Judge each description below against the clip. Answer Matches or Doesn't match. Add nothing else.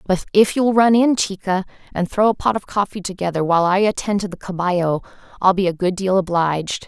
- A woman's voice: Matches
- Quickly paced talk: Matches